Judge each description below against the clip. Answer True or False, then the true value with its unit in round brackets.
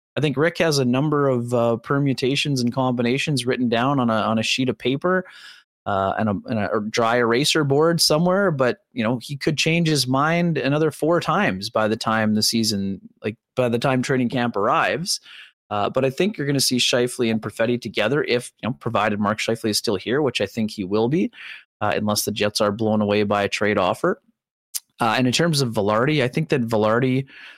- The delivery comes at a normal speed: False (220 wpm)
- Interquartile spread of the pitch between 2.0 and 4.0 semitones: False (4.6 semitones)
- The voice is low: True (125 Hz)